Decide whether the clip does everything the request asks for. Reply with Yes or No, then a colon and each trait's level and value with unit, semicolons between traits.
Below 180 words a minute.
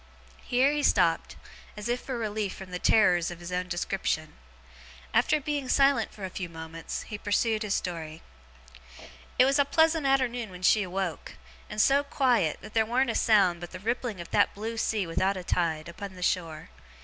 No: average, 190 wpm